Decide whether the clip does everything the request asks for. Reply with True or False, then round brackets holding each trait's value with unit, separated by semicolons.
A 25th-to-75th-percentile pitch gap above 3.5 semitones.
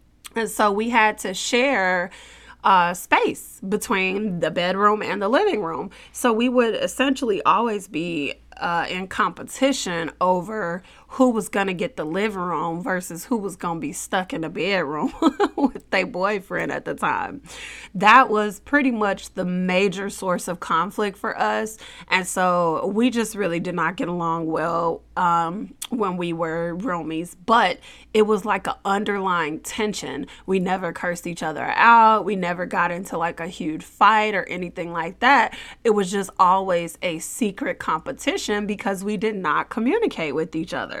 True (4.0 semitones)